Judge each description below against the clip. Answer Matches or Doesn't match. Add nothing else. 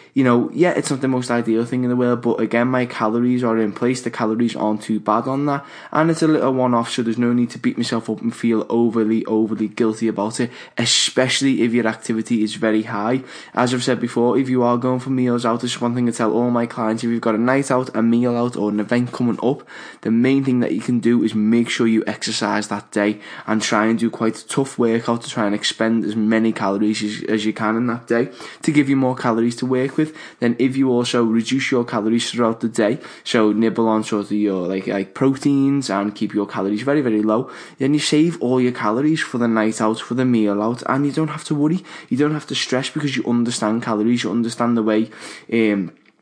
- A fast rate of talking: Matches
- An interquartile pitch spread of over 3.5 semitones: Doesn't match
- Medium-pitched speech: Doesn't match